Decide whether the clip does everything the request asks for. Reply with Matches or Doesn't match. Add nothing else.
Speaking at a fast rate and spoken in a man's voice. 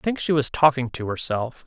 Matches